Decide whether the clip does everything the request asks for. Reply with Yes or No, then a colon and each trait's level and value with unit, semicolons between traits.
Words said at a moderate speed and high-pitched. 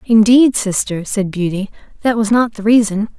Yes: average, 170 wpm; high, 215 Hz